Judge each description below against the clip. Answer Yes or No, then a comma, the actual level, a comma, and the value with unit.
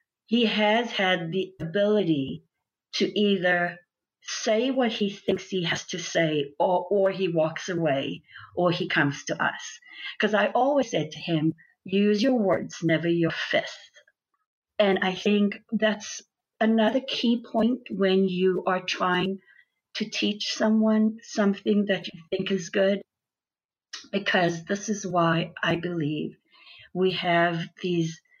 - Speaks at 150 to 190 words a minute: No, average, 140 wpm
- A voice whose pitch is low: No, high, 190 Hz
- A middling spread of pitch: Yes, average, 3.7 semitones